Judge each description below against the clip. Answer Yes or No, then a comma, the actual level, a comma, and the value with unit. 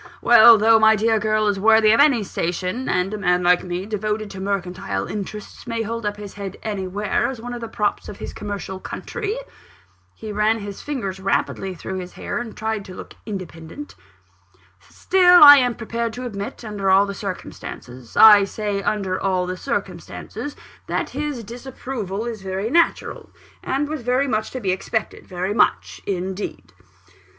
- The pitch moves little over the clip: No, average, 3.3 semitones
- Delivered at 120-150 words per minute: No, average, 175 wpm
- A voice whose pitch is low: No, high, 210 Hz